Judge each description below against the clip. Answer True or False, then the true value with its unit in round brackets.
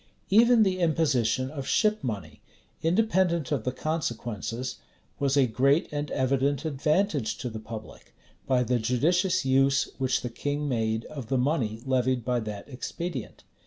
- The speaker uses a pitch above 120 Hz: True (135 Hz)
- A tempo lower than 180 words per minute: True (150 wpm)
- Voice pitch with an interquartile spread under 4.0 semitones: False (4.5 semitones)